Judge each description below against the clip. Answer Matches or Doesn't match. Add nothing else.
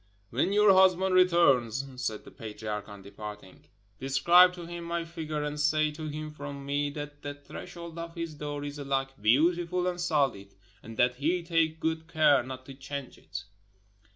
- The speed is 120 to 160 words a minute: Doesn't match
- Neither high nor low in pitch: Matches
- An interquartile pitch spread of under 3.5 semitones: Doesn't match